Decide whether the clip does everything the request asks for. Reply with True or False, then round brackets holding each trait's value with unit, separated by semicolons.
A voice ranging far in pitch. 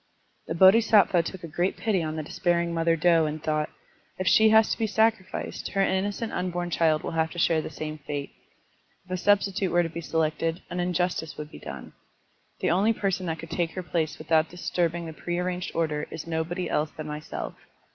False (2.6 semitones)